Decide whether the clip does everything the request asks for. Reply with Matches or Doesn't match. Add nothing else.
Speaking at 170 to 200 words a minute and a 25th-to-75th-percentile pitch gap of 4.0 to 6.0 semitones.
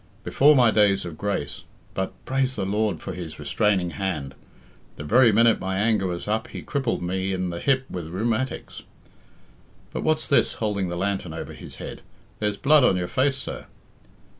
Matches